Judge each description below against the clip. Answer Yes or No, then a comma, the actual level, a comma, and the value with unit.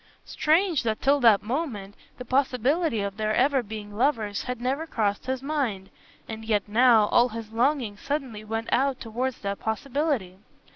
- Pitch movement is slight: No, average, 4.3 semitones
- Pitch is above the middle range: Yes, high, 235 Hz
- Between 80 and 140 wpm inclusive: No, average, 160 wpm